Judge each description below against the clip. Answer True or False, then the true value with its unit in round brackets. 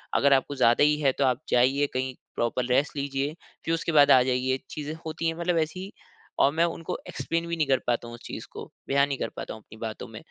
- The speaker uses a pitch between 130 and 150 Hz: True (140 Hz)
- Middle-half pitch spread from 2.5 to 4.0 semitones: True (3.5 semitones)